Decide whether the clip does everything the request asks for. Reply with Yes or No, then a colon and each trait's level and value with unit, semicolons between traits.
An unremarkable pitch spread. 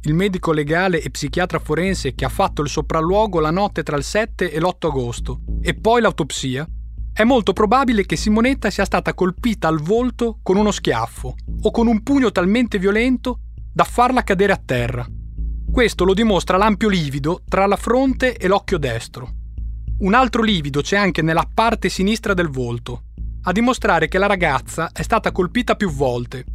No: wide, 5.8 semitones